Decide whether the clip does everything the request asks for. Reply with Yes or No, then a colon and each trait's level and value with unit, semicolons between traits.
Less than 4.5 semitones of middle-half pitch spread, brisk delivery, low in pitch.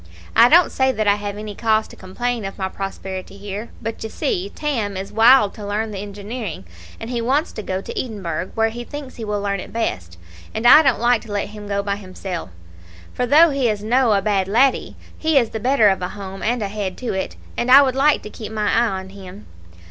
No: average, 3.5 semitones; fast, 240 wpm; high, 215 Hz